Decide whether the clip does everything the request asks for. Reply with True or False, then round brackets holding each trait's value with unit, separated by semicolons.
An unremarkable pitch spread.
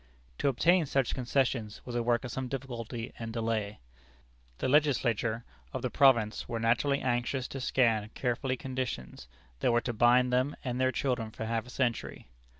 False (2.3 semitones)